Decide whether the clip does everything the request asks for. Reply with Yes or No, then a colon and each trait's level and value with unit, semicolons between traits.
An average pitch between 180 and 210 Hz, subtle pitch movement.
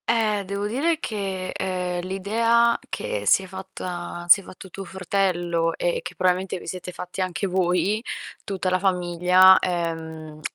Yes: medium, 185 Hz; narrow, 2.1 semitones